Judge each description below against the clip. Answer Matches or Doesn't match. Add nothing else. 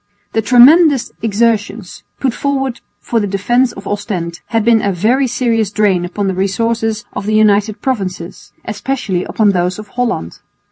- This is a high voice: Matches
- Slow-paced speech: Doesn't match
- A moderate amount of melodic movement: Matches